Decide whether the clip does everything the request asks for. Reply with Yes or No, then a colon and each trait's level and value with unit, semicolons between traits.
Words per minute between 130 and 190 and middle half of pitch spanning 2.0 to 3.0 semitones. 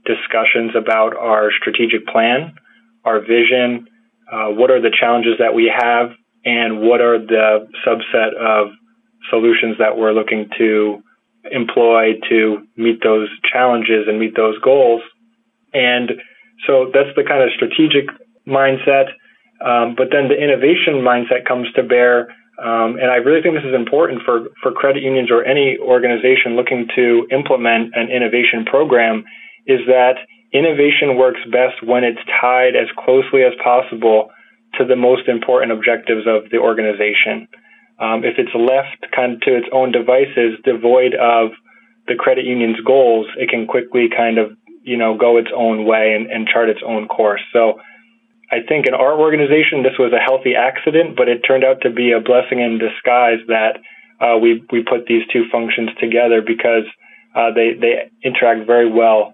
Yes: average, 165 wpm; narrow, 2.6 semitones